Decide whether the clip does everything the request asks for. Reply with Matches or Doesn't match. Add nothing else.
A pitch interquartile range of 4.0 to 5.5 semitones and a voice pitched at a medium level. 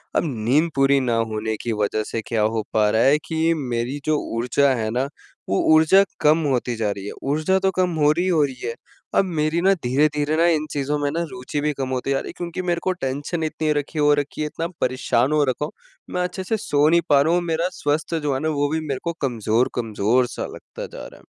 Matches